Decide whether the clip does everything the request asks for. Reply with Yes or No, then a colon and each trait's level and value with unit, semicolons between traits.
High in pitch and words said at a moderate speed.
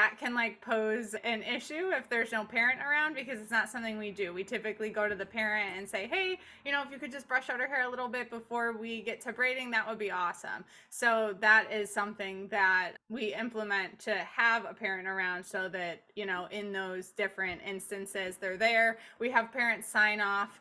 No: high, 220 Hz; fast, 215 wpm